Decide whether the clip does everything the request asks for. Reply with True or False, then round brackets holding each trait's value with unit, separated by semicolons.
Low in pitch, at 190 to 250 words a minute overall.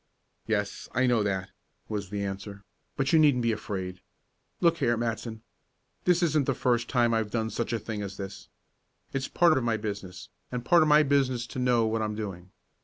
True (115 Hz; 195 wpm)